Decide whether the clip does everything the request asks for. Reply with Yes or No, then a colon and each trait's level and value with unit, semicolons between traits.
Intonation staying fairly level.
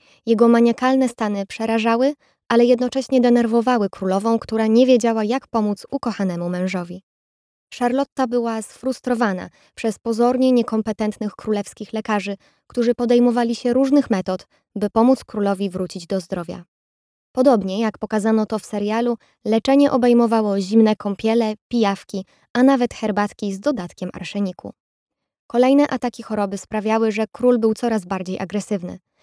No: average, 3.0 semitones